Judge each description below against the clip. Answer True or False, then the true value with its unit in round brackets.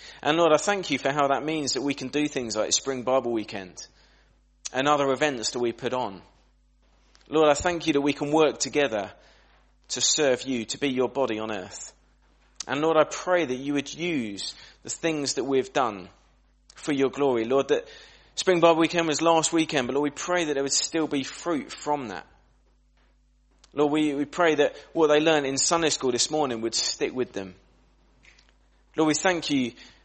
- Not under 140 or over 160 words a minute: False (200 wpm)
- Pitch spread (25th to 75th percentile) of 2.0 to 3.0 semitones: False (3.6 semitones)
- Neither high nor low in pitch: True (145 Hz)